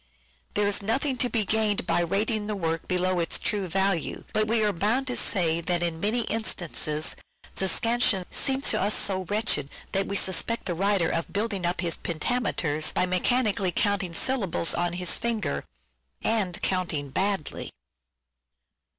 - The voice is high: Yes, high, 195 Hz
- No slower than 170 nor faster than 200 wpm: No, average, 160 wpm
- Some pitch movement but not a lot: Yes, average, 3.8 semitones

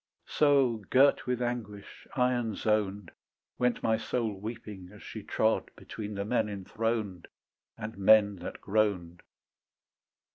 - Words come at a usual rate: No, slow, 120 wpm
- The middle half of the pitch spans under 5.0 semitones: Yes, average, 3.0 semitones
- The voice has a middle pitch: No, low, 110 Hz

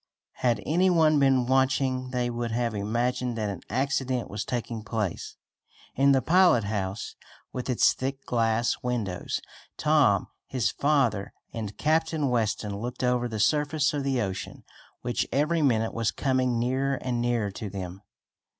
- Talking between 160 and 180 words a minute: No, average, 150 wpm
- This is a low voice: Yes, low, 125 Hz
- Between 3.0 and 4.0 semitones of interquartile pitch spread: Yes, average, 3.3 semitones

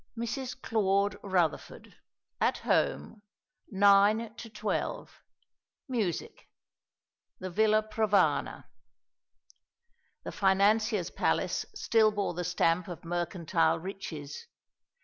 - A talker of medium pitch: No, high, 200 Hz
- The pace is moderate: No, slow, 90 wpm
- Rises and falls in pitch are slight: No, average, 3.5 semitones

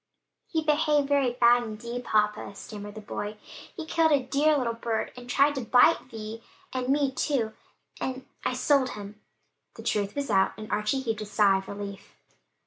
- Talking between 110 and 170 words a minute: No, average, 180 wpm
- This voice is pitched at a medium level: No, high, 240 Hz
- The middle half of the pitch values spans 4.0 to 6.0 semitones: Yes, average, 4.7 semitones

